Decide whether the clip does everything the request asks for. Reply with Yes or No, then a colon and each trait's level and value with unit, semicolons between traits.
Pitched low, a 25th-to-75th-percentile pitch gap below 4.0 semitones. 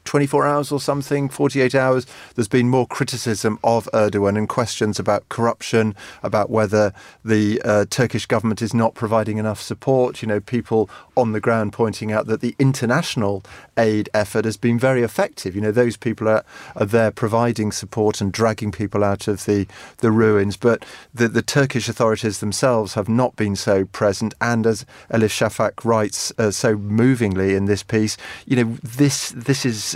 Yes: low, 115 Hz; narrow, 2.6 semitones